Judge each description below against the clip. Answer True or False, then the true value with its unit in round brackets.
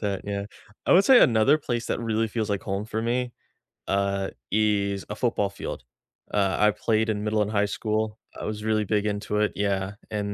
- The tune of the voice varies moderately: False (1.6 semitones)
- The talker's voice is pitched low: True (105 Hz)